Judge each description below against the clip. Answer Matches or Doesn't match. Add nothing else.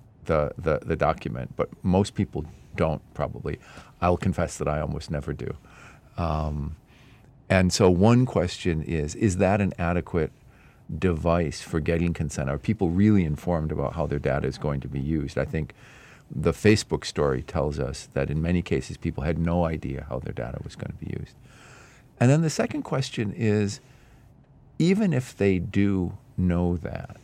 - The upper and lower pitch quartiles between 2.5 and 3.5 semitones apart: Doesn't match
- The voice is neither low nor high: Doesn't match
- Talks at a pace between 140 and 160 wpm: Doesn't match